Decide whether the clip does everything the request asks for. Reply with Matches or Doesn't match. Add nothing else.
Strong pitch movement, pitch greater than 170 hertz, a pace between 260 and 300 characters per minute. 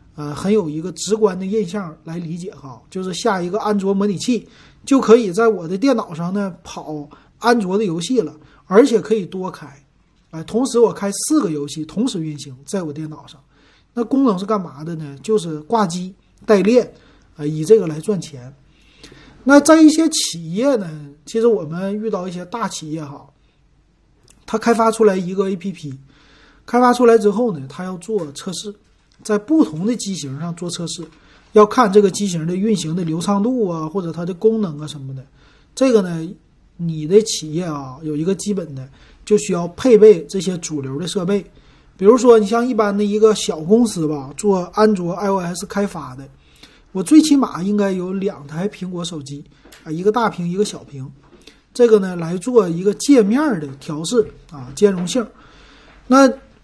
Matches